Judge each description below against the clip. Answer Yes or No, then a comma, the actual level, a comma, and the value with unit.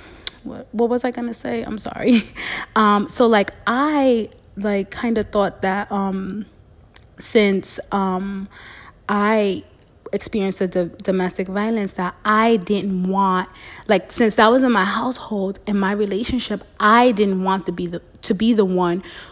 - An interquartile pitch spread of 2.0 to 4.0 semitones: Yes, average, 2.9 semitones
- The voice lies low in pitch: No, high, 205 Hz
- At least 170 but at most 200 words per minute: No, average, 155 wpm